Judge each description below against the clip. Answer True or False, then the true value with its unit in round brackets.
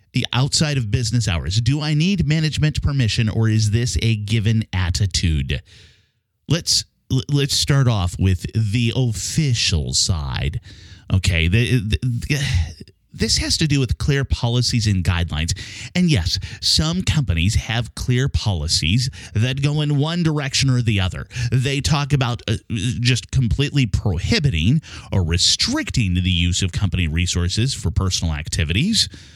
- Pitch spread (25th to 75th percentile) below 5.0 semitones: False (5.6 semitones)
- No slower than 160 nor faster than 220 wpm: False (140 wpm)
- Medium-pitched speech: False (110 Hz)